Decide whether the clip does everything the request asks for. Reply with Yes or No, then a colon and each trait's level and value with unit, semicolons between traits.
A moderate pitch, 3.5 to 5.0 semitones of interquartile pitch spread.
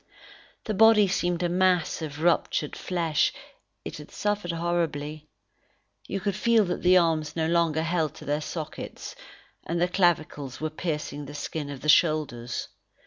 No: medium, 165 Hz; average, 2.9 semitones